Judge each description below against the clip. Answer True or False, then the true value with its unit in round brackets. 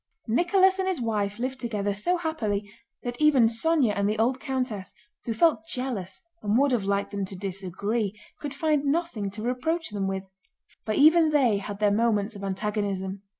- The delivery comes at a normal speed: True (180 wpm)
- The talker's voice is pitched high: True (225 Hz)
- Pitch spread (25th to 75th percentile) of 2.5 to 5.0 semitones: False (5.6 semitones)